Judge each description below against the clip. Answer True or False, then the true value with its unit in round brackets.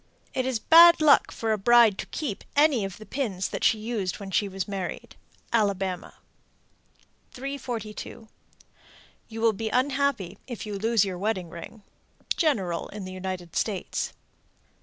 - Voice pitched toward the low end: False (215 Hz)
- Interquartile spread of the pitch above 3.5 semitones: True (4.2 semitones)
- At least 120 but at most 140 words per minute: False (150 wpm)